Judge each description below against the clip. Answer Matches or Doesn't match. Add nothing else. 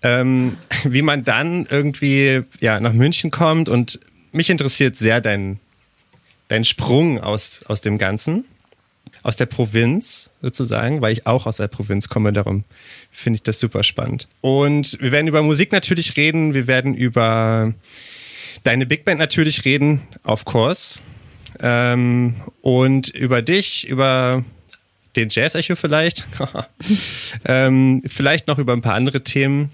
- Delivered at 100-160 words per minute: Matches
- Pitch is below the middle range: Matches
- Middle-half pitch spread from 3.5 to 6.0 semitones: Matches